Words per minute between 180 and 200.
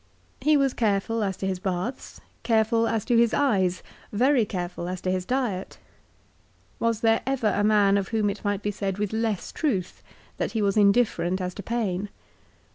Yes: average, 185 wpm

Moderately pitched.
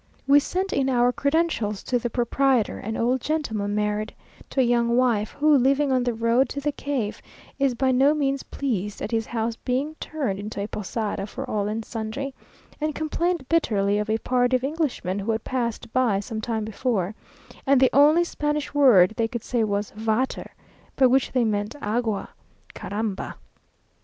No: high, 245 Hz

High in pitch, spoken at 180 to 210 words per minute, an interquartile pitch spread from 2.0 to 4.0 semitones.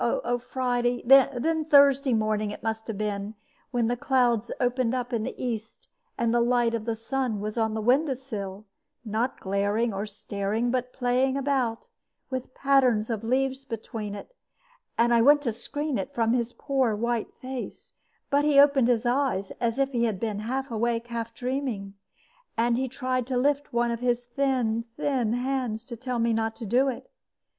Yes: high, 240 Hz; average, 185 wpm; average, 2.7 semitones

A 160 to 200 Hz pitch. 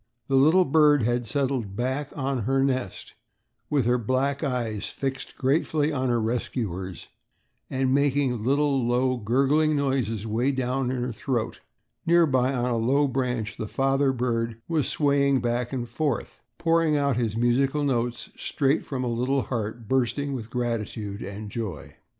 No: low, 130 Hz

